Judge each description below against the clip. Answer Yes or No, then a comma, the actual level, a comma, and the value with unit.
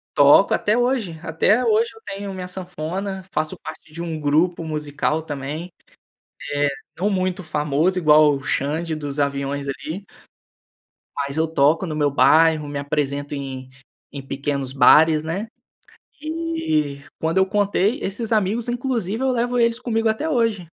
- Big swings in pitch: Yes, wide, 5.9 semitones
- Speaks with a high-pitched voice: No, medium, 165 Hz